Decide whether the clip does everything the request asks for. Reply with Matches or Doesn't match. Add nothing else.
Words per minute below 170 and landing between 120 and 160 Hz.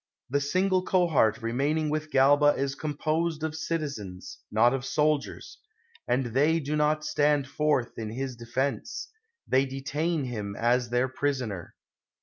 Matches